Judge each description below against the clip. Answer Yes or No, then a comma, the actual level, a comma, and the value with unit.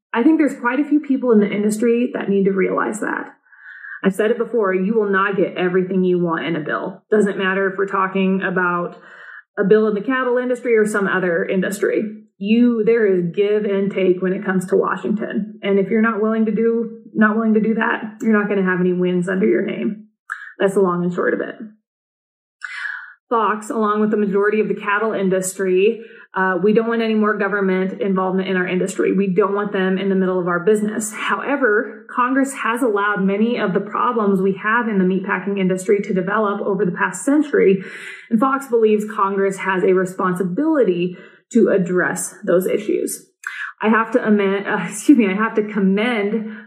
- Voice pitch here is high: Yes, high, 205 Hz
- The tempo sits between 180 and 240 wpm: Yes, average, 200 wpm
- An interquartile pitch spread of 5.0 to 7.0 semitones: No, average, 2.7 semitones